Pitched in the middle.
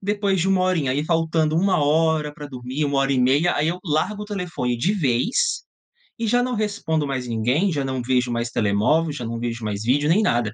Yes: medium, 150 Hz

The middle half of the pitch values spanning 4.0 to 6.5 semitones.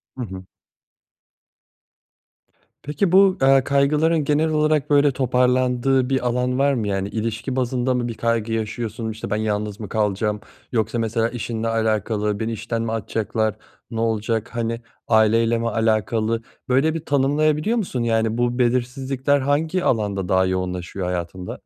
No: average, 3.4 semitones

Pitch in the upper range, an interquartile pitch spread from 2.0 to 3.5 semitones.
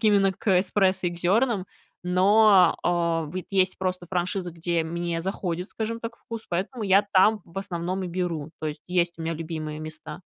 No: medium, 180 Hz; narrow, 2.5 semitones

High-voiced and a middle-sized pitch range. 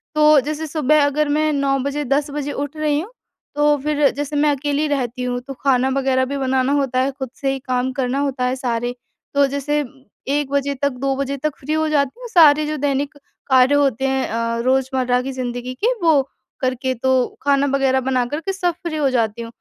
No: very high, 275 Hz; narrow, 2.2 semitones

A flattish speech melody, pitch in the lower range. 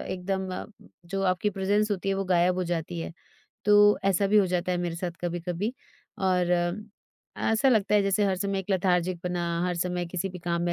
No: narrow, 1.9 semitones; medium, 185 Hz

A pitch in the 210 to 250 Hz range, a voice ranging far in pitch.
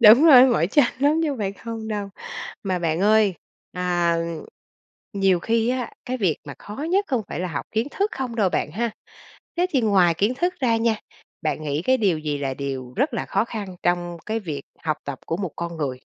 No: high, 200 Hz; wide, 5.8 semitones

